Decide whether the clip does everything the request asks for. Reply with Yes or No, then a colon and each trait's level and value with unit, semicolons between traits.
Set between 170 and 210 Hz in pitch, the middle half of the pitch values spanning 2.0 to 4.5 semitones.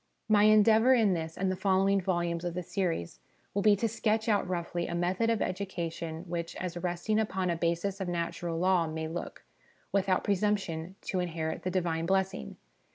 Yes: medium, 185 Hz; average, 2.8 semitones